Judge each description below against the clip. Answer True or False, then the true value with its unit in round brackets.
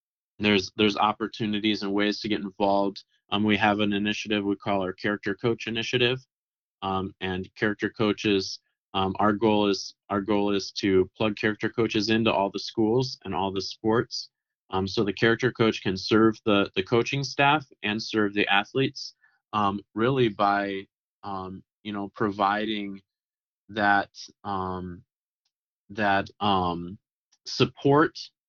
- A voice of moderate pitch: False (105 Hz)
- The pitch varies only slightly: True (1.9 semitones)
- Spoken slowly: False (145 wpm)